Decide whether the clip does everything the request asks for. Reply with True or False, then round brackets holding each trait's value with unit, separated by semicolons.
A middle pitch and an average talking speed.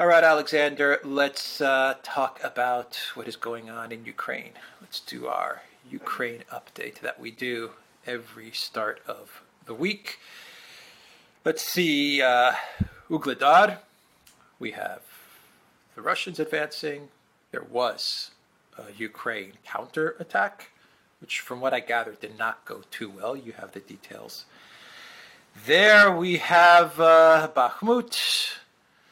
False (155 Hz; 125 wpm)